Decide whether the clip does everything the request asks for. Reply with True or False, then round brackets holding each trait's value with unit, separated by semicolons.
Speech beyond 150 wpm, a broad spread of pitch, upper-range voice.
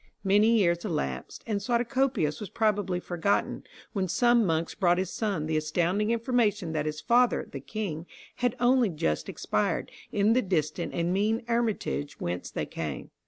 True (160 wpm; 5.9 semitones; 195 Hz)